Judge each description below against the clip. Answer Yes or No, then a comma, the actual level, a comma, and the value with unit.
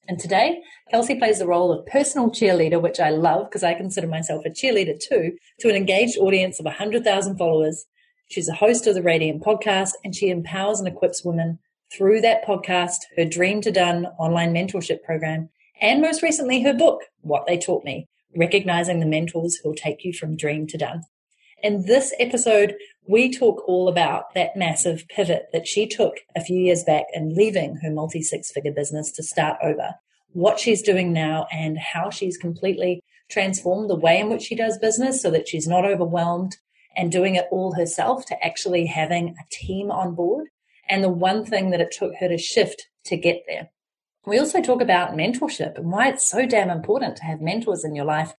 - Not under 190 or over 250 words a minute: Yes, average, 195 wpm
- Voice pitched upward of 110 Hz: Yes, medium, 185 Hz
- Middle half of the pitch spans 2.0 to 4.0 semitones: No, average, 4.4 semitones